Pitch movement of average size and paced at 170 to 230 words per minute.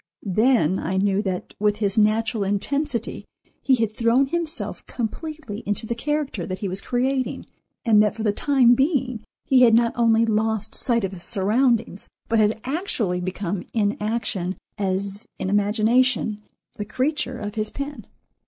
No: average, 3.8 semitones; average, 160 wpm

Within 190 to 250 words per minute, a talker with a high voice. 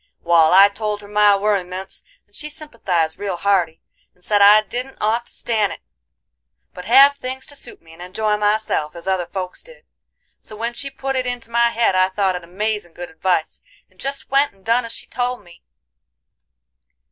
Yes: average, 195 wpm; high, 210 Hz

